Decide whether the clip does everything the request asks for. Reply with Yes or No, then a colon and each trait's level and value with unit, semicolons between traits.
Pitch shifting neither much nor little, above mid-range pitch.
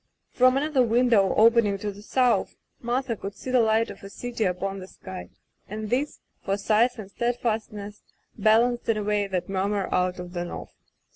Yes: average, 3.4 semitones; high, 215 Hz